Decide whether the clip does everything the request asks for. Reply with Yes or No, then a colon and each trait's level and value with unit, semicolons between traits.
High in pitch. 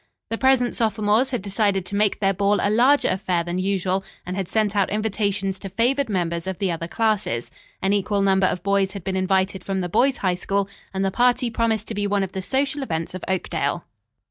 Yes: high, 200 Hz